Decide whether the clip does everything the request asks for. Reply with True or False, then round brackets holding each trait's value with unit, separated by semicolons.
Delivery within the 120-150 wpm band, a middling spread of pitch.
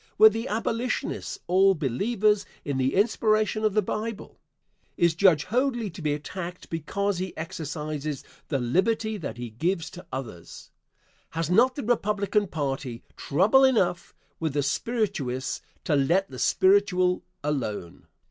False (140 wpm; 6.4 semitones)